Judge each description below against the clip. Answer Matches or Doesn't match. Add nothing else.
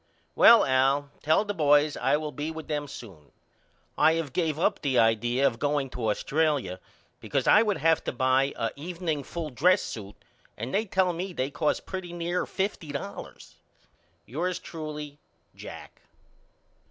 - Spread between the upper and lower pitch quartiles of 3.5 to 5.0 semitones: Matches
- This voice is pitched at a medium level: Matches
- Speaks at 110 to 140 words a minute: Doesn't match